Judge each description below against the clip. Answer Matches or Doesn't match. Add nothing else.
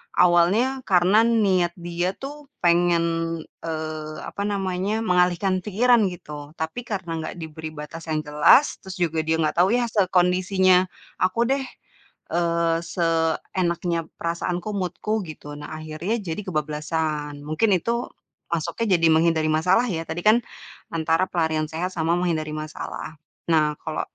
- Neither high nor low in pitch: Matches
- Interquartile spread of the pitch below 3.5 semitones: Matches